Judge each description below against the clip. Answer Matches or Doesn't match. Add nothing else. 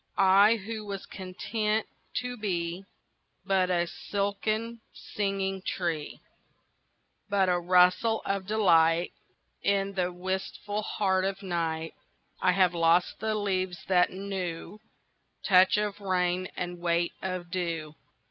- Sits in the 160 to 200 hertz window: Matches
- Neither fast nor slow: Doesn't match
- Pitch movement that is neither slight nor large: Doesn't match